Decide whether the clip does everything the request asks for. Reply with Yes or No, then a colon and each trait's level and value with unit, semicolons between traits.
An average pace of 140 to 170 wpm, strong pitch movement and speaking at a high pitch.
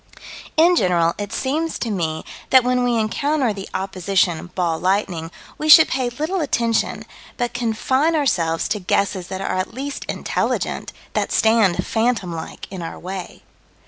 Yes: average, 155 wpm; wide, 6.1 semitones; high, 215 Hz